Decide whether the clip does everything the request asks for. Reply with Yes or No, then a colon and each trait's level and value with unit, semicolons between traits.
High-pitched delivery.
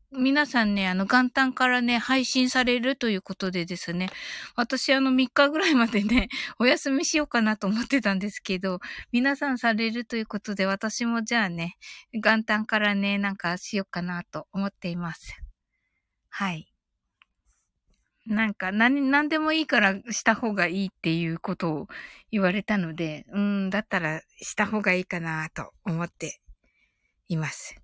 Yes: high, 210 Hz